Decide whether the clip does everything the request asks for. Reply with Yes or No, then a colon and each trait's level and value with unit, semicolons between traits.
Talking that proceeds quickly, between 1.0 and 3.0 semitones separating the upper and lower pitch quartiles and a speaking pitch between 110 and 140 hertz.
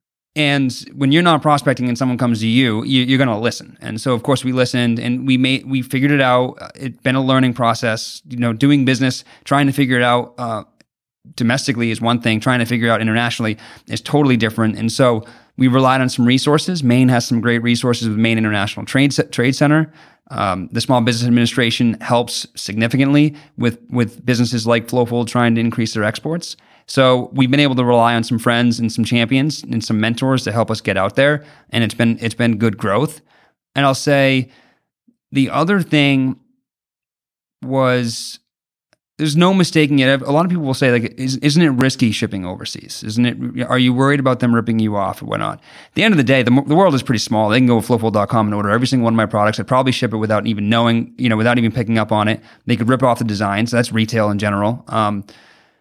Yes: fast, 225 wpm; narrow, 2.6 semitones; low, 120 Hz